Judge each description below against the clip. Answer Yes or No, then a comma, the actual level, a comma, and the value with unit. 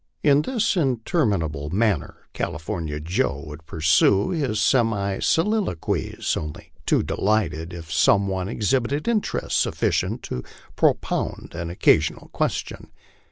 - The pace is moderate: No, slow, 120 wpm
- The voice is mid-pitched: No, low, 100 Hz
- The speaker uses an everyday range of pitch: No, wide, 8.2 semitones